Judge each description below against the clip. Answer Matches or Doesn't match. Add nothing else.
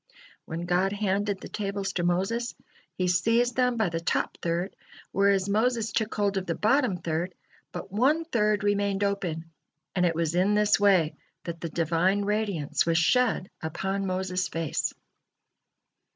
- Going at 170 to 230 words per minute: Doesn't match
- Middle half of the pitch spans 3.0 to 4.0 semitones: Matches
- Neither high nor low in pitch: Doesn't match